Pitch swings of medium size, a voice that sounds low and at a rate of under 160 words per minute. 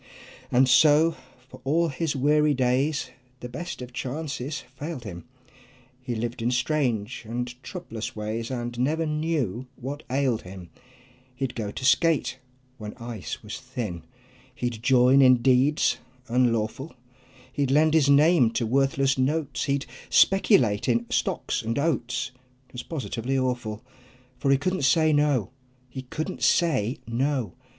Yes: average, 3.7 semitones; low, 130 Hz; average, 140 wpm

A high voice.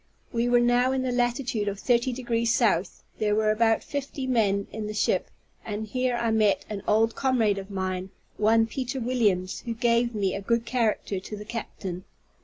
Yes: high, 225 Hz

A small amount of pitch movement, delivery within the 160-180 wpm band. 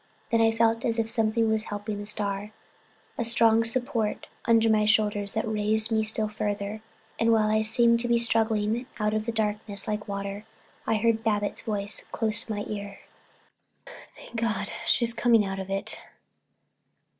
Yes: narrow, 1.6 semitones; average, 170 wpm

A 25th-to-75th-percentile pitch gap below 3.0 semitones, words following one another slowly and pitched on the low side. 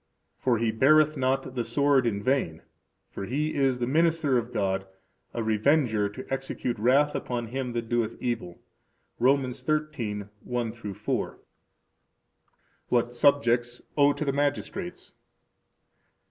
No: average, 3.7 semitones; slow, 125 wpm; low, 125 Hz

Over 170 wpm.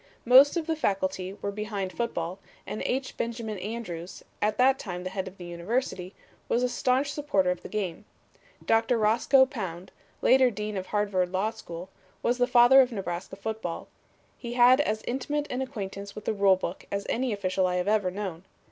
Yes: average, 185 wpm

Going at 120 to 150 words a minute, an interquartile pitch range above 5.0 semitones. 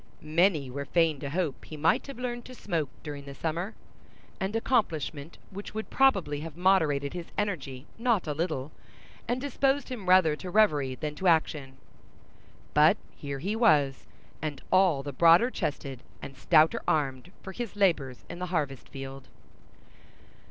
No: average, 160 wpm; wide, 5.5 semitones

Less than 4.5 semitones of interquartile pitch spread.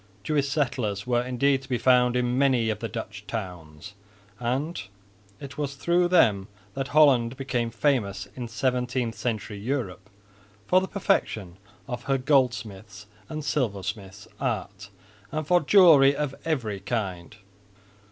No: average, 4.8 semitones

